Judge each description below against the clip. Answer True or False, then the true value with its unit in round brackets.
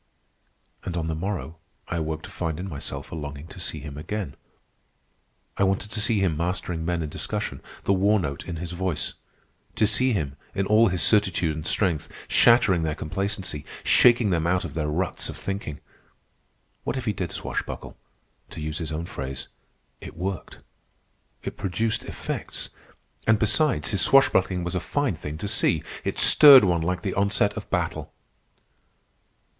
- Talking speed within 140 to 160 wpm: False (170 wpm)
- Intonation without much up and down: False (4.5 semitones)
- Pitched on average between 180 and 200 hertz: False (90 Hz)